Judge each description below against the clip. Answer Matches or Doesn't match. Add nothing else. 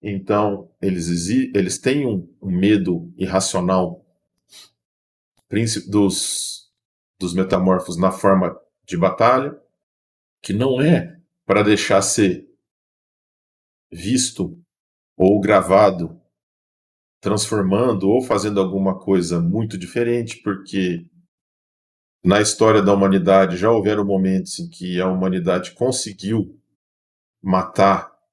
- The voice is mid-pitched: Doesn't match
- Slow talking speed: Matches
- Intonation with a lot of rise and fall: Doesn't match